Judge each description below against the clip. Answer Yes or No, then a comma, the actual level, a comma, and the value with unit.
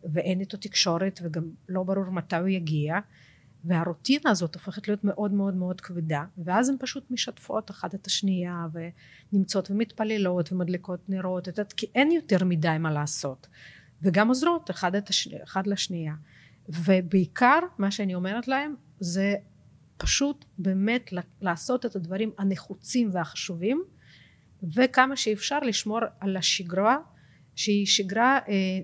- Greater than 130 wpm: No, average, 125 wpm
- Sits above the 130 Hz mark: Yes, high, 190 Hz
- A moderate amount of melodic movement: Yes, average, 3.5 semitones